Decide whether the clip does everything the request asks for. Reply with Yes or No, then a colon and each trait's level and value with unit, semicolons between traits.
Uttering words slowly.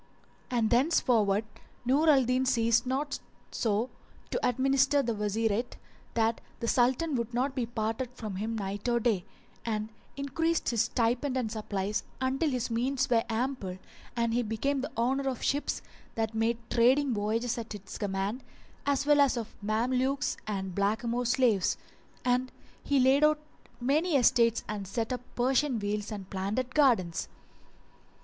No: average, 150 wpm